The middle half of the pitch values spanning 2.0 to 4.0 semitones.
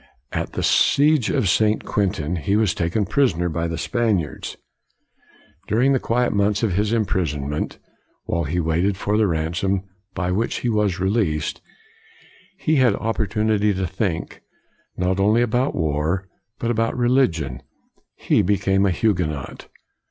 No: average, 4.5 semitones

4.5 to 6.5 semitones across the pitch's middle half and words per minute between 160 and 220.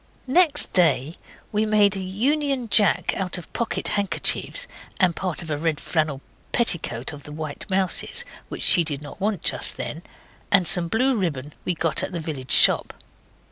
Yes: average, 5.2 semitones; average, 175 wpm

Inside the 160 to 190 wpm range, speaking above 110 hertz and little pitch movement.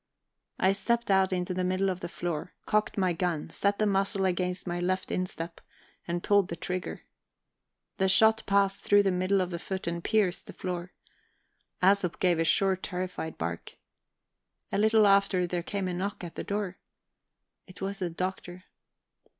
Yes: average, 175 wpm; medium, 185 Hz; narrow, 1.9 semitones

